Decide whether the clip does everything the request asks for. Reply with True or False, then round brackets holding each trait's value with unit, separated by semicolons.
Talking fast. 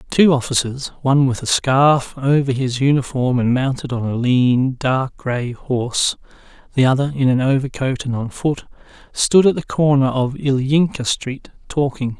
False (160 wpm)